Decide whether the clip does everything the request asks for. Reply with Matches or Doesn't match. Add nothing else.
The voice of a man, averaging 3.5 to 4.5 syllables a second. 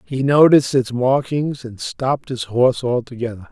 Doesn't match